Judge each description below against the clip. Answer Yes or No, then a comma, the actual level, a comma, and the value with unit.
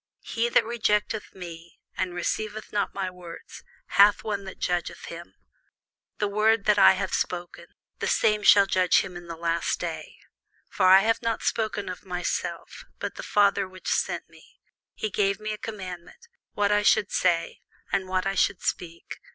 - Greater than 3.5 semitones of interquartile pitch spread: No, average, 2.7 semitones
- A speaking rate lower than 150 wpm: No, average, 175 wpm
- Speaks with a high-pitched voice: Yes, high, 195 Hz